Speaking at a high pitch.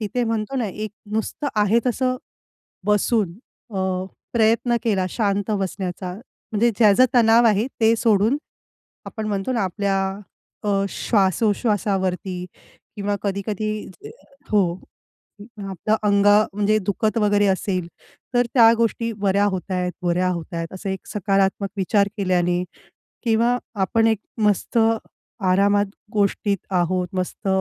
Yes: high, 205 Hz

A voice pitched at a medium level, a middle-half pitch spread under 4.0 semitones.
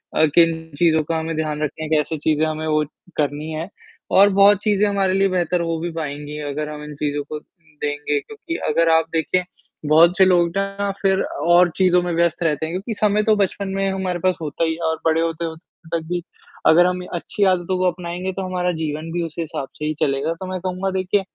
Yes: medium, 170 Hz; average, 2.9 semitones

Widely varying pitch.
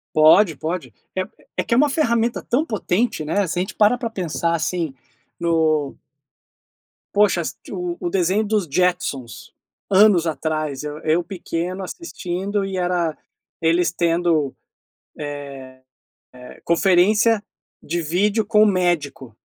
No: average, 4.1 semitones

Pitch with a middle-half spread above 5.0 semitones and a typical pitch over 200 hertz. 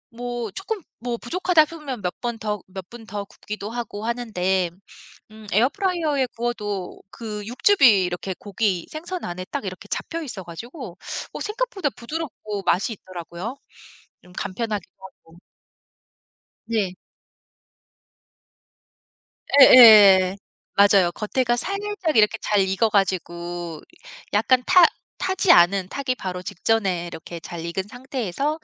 Yes: wide, 5.5 semitones; high, 215 Hz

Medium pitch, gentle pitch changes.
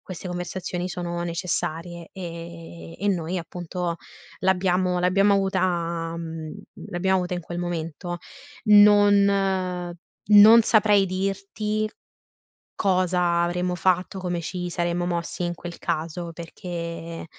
Yes: medium, 175 Hz; narrow, 1.8 semitones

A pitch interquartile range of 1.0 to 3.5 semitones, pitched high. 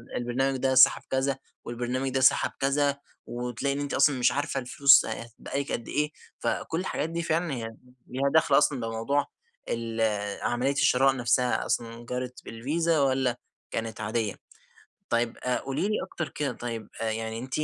No: average, 2.9 semitones; low, 130 Hz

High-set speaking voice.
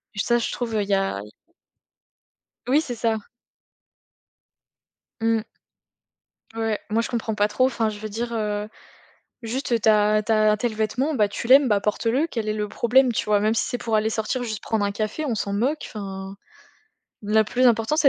Yes: high, 220 Hz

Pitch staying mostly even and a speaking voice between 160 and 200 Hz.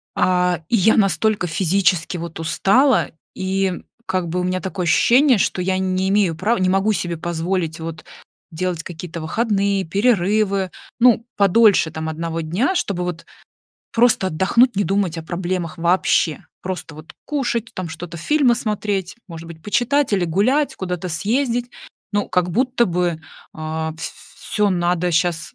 No: average, 3.6 semitones; medium, 185 Hz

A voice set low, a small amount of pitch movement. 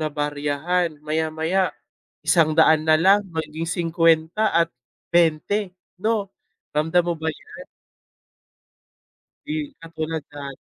No: medium, 160 Hz; narrow, 1.8 semitones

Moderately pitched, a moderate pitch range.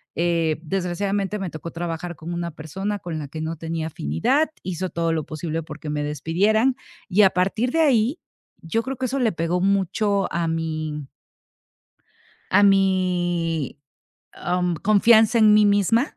Yes: medium, 175 Hz; average, 3.9 semitones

